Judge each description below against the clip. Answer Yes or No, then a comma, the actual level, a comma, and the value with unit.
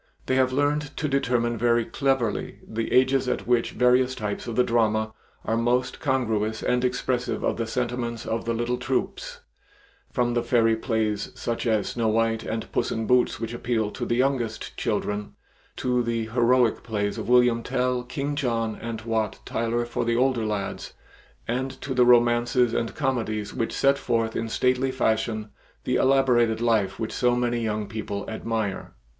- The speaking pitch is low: Yes, low, 120 Hz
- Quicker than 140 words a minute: Yes, average, 170 wpm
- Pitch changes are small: Yes, narrow, 2.0 semitones